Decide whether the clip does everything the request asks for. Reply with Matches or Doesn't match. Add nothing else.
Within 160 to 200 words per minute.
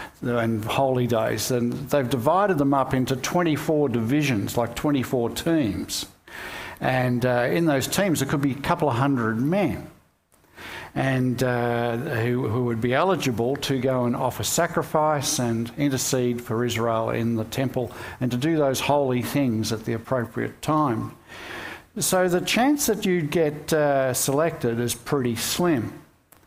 Doesn't match